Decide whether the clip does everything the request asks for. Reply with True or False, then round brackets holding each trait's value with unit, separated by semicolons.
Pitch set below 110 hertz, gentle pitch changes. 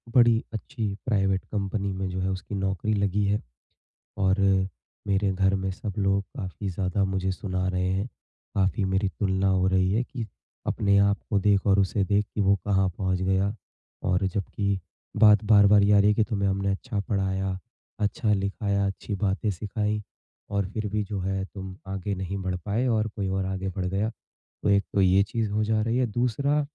True (100 Hz; 1.6 semitones)